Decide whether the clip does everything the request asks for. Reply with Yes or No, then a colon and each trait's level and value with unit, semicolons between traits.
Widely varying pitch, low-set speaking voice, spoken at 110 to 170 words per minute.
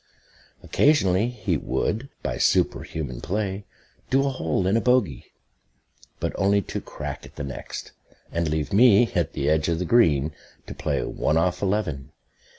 Yes: wide, 5.7 semitones; very low, 95 Hz; average, 155 wpm